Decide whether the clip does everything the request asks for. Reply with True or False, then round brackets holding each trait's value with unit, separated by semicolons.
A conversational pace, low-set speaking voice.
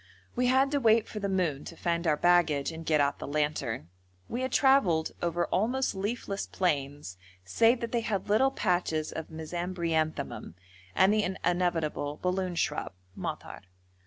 False (160 wpm; 175 Hz)